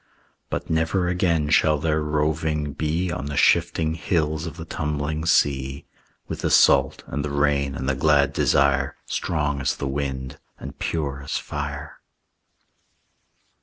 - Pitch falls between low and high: No, very low, 75 Hz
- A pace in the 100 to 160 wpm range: Yes, average, 145 wpm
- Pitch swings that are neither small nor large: No, narrow, 2.0 semitones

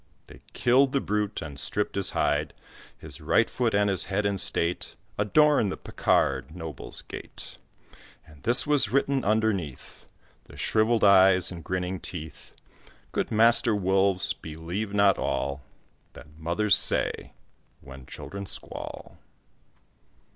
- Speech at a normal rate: No, slow, 130 wpm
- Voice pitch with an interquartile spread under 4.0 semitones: No, average, 4.4 semitones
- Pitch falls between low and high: No, low, 100 Hz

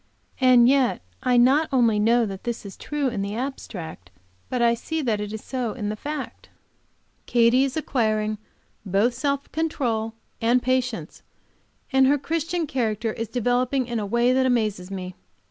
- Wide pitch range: No, average, 3.5 semitones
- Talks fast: No, average, 165 wpm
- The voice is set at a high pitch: Yes, high, 240 Hz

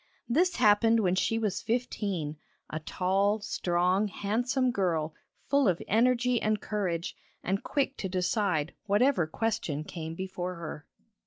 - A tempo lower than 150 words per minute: Yes, slow, 135 wpm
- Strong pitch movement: No, average, 4.5 semitones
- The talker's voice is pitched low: No, high, 200 Hz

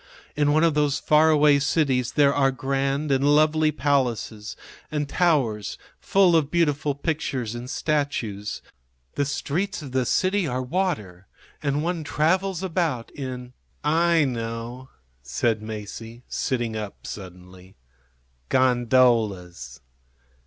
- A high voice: No, low, 135 Hz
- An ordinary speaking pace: No, slow, 125 wpm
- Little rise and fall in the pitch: No, average, 4.9 semitones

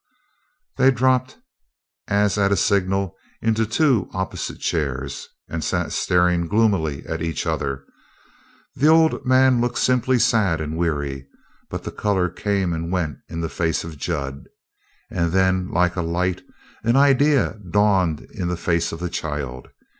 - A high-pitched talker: No, very low, 90 Hz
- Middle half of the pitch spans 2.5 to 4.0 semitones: No, average, 5.3 semitones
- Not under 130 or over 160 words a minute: Yes, average, 150 wpm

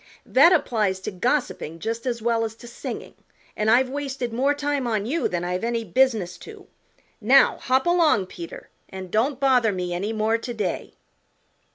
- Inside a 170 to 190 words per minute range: Yes, average, 175 wpm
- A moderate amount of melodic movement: Yes, average, 4.5 semitones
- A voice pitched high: Yes, high, 230 Hz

